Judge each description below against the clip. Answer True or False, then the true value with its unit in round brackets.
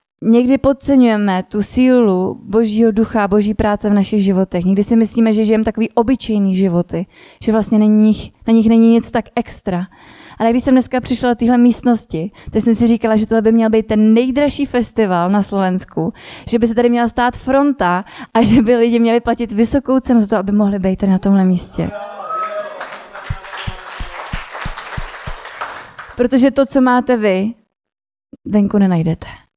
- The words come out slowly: False (165 wpm)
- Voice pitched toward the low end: False (225 Hz)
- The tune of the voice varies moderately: True (3.0 semitones)